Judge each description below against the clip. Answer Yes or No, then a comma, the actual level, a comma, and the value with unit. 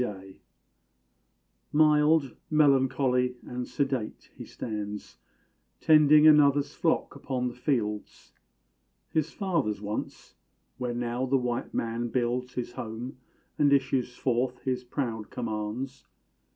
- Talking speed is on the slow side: Yes, slow, 110 wpm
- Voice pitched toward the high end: No, low, 125 Hz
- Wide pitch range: No, average, 3.0 semitones